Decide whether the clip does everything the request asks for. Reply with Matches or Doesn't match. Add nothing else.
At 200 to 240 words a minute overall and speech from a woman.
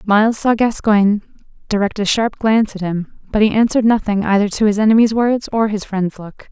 Matches